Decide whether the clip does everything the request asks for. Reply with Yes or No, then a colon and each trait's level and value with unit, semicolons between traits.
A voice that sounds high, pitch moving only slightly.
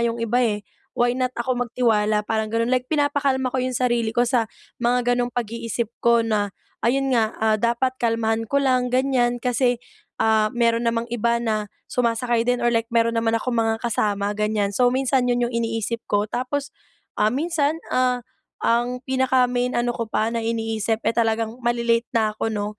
Yes: high, 235 Hz; narrow, 1.8 semitones